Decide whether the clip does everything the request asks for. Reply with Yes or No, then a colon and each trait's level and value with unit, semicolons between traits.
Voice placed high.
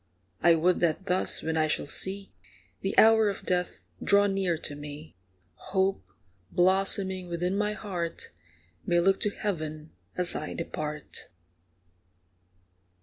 No: medium, 180 Hz